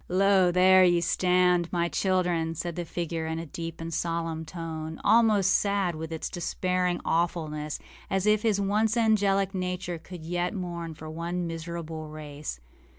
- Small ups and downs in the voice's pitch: Yes, narrow, 2.2 semitones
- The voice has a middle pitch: Yes, medium, 175 Hz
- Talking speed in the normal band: Yes, average, 155 wpm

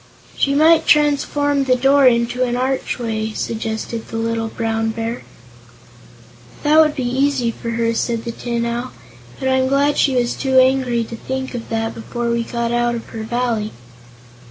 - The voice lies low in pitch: No, high, 240 Hz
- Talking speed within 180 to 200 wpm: No, average, 170 wpm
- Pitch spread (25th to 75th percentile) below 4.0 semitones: Yes, narrow, 2.5 semitones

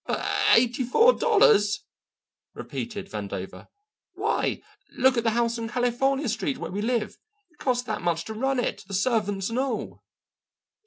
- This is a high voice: Yes, high, 230 Hz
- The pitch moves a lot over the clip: No, average, 3.6 semitones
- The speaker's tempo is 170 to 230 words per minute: No, average, 155 wpm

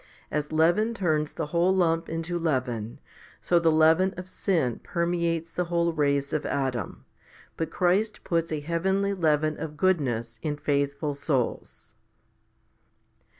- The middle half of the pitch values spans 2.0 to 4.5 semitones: Yes, average, 3.0 semitones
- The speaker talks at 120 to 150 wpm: Yes, average, 140 wpm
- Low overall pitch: No, medium, 160 Hz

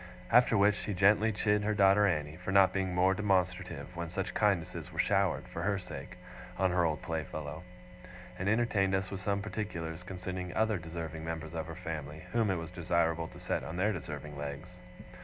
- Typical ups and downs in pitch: Yes, average, 3.4 semitones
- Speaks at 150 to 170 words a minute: No, average, 190 wpm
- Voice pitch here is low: Yes, very low, 90 Hz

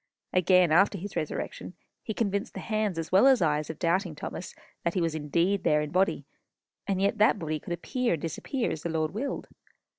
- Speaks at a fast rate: Yes, fast, 210 wpm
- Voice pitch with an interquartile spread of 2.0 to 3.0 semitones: No, average, 4.1 semitones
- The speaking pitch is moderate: Yes, medium, 180 Hz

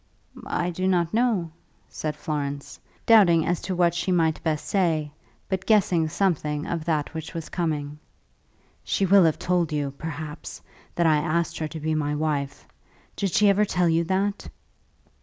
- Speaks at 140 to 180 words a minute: Yes, average, 165 wpm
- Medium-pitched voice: Yes, medium, 165 Hz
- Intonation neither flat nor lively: Yes, average, 3.1 semitones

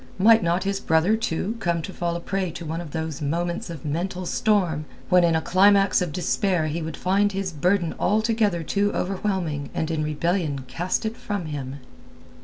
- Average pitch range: Yes, average, 3.5 semitones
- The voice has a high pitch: No, medium, 175 Hz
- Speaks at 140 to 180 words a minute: No, average, 190 wpm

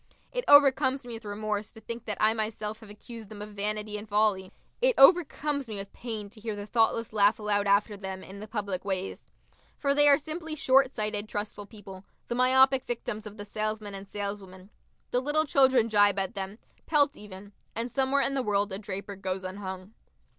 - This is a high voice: Yes, high, 215 Hz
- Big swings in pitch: No, average, 3.7 semitones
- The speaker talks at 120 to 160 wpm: No, average, 195 wpm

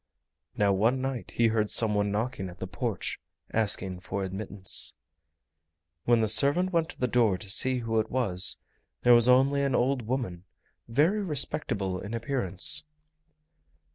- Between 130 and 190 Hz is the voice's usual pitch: No, low, 115 Hz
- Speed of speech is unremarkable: Yes, average, 155 wpm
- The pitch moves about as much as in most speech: Yes, average, 4.5 semitones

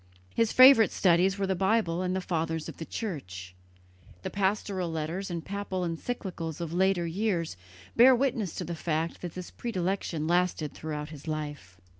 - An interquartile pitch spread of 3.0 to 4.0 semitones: Yes, average, 3.4 semitones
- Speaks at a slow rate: No, average, 165 wpm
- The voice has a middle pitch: Yes, medium, 175 Hz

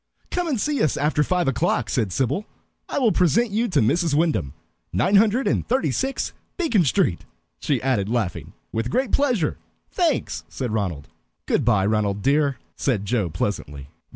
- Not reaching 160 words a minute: No, average, 165 wpm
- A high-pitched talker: No, medium, 140 Hz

